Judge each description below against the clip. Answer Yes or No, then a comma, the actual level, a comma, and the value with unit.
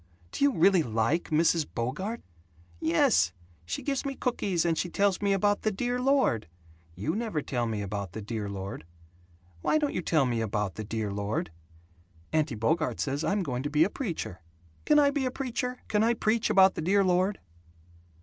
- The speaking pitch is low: No, medium, 165 Hz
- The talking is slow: No, average, 190 wpm